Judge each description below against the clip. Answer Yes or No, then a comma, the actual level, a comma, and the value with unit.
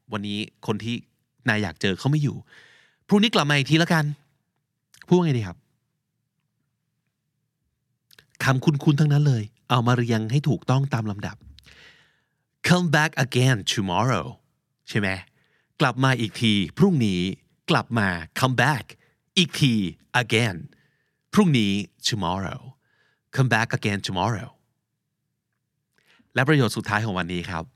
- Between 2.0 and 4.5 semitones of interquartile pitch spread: No, average, 5.2 semitones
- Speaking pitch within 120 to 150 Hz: Yes, low, 130 Hz